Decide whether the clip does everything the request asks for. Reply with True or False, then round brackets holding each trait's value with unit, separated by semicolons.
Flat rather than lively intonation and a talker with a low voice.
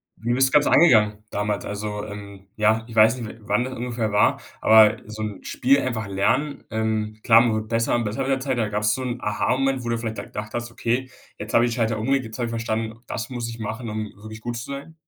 True (2.2 semitones; 115 Hz)